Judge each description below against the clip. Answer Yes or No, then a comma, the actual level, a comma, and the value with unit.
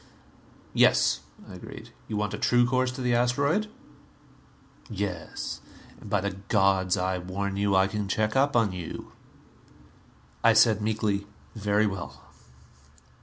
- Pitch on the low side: Yes, low, 105 Hz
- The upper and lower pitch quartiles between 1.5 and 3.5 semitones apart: Yes, average, 3.2 semitones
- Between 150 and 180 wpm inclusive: No, slow, 135 wpm